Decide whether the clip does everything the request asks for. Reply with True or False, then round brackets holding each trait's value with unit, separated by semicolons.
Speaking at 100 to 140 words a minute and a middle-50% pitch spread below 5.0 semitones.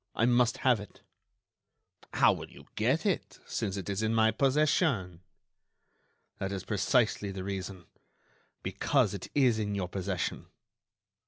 True (135 wpm; 3.9 semitones)